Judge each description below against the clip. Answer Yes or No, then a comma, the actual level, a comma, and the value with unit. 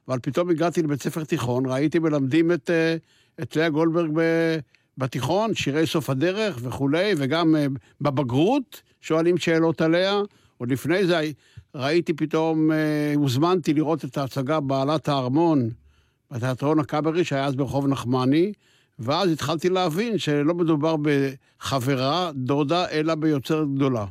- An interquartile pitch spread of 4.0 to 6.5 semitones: No, average, 3.3 semitones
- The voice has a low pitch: No, medium, 155 Hz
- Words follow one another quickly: No, average, 120 wpm